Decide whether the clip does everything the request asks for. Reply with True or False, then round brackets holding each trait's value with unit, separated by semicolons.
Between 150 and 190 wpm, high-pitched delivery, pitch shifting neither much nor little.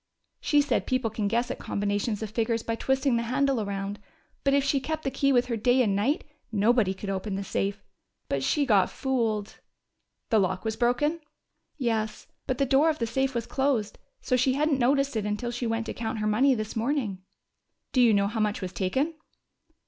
False (205 wpm; 230 Hz; 4.2 semitones)